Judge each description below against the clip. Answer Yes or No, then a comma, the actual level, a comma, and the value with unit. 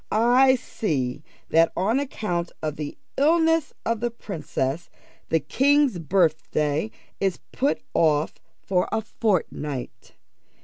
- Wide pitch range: Yes, wide, 7.9 semitones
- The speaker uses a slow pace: Yes, slow, 115 wpm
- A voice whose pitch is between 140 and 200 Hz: Yes, high, 190 Hz